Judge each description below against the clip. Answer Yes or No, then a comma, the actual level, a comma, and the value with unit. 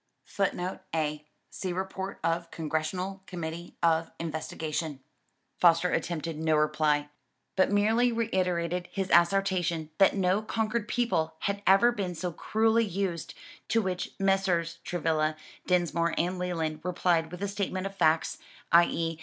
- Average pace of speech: No, slow, 130 wpm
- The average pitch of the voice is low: No, medium, 175 Hz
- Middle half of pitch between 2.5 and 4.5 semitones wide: Yes, average, 3.1 semitones